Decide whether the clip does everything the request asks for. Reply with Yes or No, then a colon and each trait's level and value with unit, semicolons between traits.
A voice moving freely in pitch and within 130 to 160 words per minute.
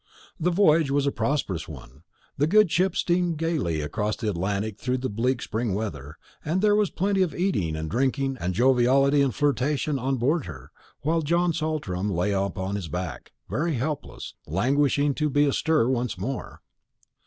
No: wide, 7.5 semitones; average, 170 wpm